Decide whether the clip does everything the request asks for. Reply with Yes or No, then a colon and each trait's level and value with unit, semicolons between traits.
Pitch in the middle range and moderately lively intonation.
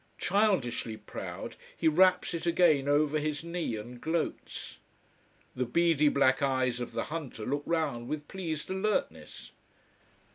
Yes: medium, 150 Hz; average, 4.5 semitones